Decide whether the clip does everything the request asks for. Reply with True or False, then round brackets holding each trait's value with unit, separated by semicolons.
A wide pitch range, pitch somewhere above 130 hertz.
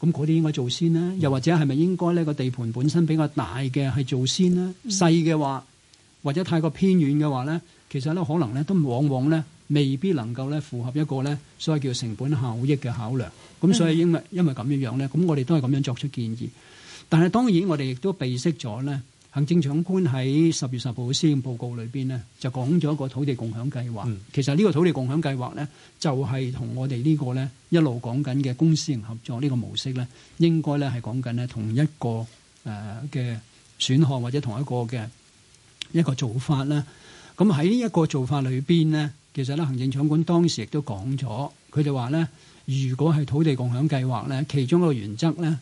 False (3.9 semitones; 140 Hz)